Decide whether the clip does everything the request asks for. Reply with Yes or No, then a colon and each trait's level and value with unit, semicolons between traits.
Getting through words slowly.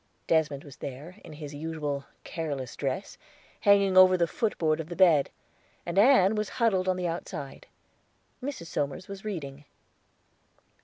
No: average, 145 wpm